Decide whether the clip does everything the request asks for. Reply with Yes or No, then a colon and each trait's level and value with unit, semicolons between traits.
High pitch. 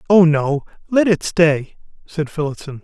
No: medium, 160 Hz